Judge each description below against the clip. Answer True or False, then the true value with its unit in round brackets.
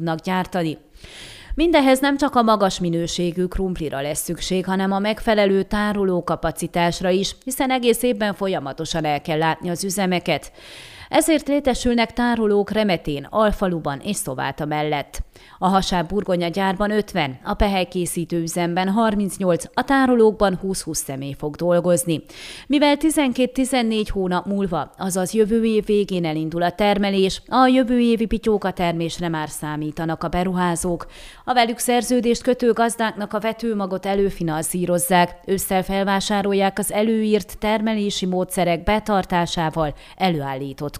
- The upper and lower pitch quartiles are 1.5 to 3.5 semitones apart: False (4.1 semitones)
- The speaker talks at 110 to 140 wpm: True (125 wpm)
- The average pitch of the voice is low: False (190 Hz)